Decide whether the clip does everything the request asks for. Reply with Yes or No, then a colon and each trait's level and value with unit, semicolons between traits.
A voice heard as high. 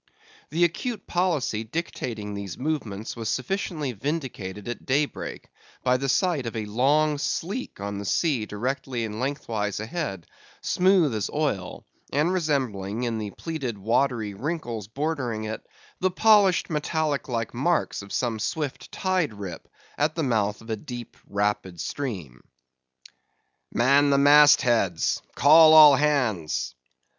No: low, 130 Hz